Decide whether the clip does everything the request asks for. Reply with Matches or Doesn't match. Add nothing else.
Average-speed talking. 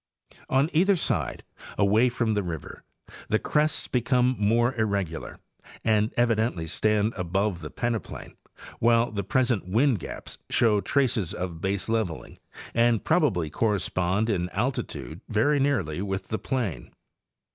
Doesn't match